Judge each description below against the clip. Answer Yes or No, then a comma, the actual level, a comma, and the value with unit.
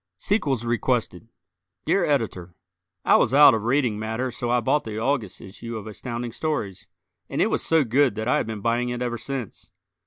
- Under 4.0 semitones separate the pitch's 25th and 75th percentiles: Yes, average, 3.4 semitones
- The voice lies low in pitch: Yes, low, 120 Hz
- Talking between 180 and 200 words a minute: Yes, average, 190 wpm